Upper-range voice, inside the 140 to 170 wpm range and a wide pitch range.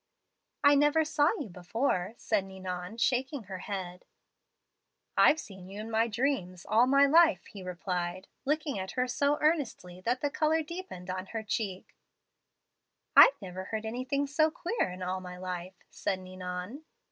Yes: high, 215 Hz; average, 160 wpm; wide, 7.4 semitones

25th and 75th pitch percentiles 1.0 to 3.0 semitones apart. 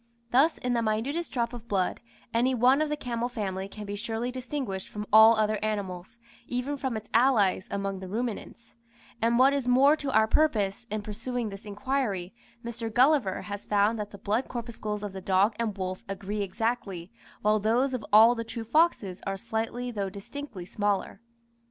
No: average, 3.5 semitones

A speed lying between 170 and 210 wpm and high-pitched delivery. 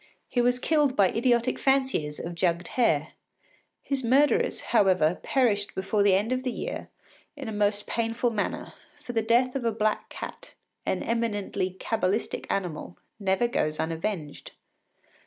No: average, 150 wpm; high, 220 Hz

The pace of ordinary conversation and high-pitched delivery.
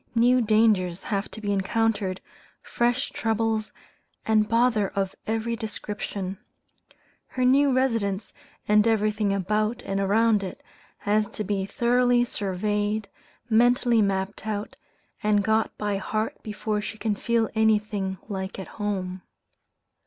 No: slow, 125 wpm; high, 215 Hz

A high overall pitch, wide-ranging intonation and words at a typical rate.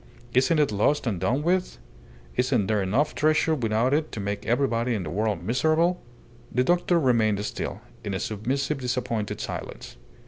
No: low, 125 Hz; wide, 5.7 semitones; average, 165 wpm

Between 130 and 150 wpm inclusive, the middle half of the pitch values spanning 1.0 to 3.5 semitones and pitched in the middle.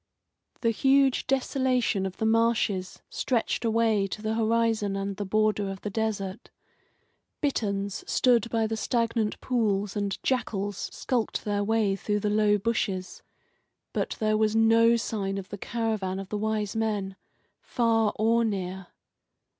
No: average, 140 wpm; narrow, 2.4 semitones; high, 215 Hz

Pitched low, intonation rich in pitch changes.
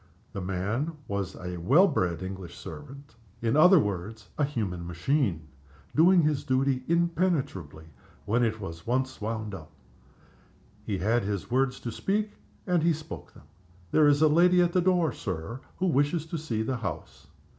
Yes: low, 125 Hz; wide, 8.2 semitones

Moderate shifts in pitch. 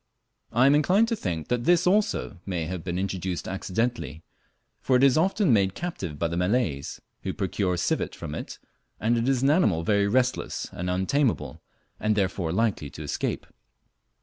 No: wide, 6.8 semitones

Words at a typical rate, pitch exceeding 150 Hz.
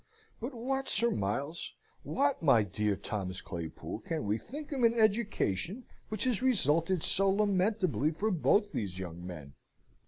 Yes: average, 150 wpm; medium, 185 Hz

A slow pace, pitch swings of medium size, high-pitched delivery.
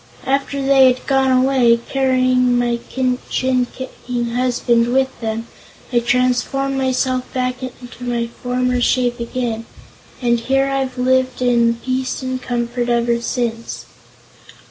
No: slow, 125 wpm; narrow, 1.5 semitones; very high, 250 Hz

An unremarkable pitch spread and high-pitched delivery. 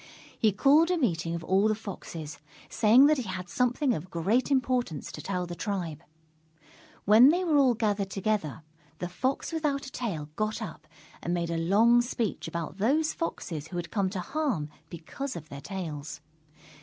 No: wide, 6.8 semitones; high, 200 Hz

